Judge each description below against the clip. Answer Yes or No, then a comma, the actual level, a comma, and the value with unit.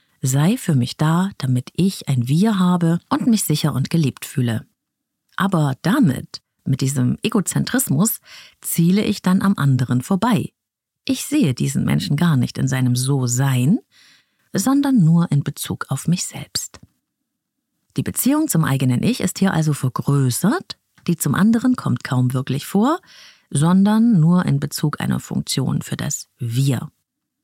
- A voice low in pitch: No, medium, 165 Hz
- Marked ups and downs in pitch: Yes, wide, 6.9 semitones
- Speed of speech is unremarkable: Yes, average, 150 wpm